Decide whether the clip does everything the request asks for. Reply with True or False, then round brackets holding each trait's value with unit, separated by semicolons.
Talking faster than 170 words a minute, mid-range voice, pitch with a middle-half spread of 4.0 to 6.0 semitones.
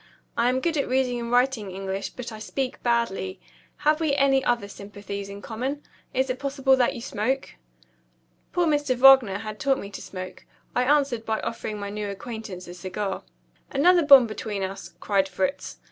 False (180 wpm; 235 Hz; 5.0 semitones)